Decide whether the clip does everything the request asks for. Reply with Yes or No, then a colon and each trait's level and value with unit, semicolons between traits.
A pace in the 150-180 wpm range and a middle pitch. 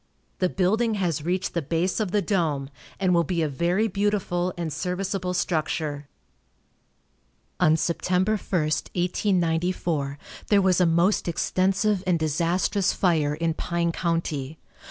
No: slow, 135 wpm; medium, 175 Hz